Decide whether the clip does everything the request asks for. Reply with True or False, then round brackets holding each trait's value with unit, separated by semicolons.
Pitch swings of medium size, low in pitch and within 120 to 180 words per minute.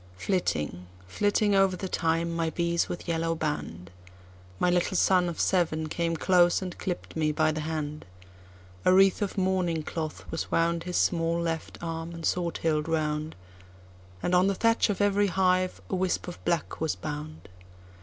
False (3.2 semitones; 165 Hz; 155 wpm)